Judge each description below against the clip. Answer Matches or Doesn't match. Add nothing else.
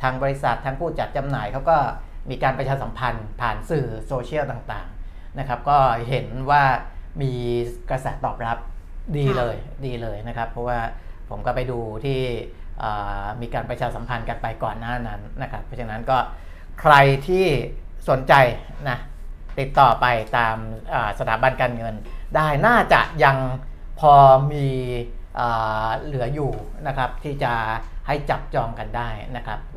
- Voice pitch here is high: Doesn't match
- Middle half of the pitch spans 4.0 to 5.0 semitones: Doesn't match